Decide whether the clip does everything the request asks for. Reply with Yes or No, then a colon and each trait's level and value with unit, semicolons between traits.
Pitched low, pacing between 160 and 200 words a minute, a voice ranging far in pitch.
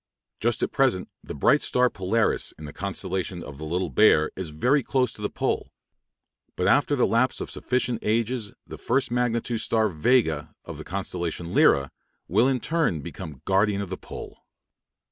Yes: low, 105 Hz; average, 180 wpm; wide, 6.2 semitones